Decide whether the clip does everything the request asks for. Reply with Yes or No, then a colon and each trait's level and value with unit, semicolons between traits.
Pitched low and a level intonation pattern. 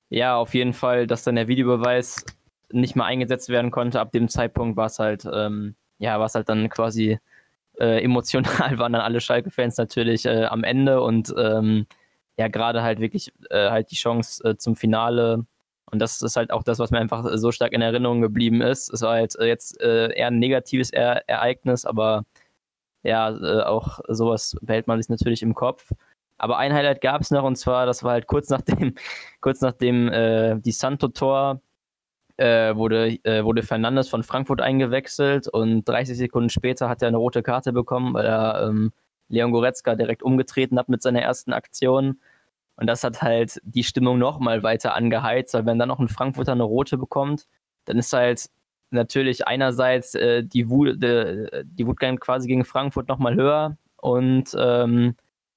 Yes: low, 120 Hz; narrow, 2.1 semitones